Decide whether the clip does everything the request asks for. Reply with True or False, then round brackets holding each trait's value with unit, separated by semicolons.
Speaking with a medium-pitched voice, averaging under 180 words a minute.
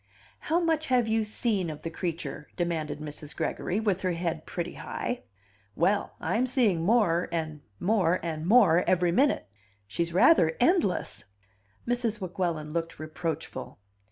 True (175 Hz; 140 wpm)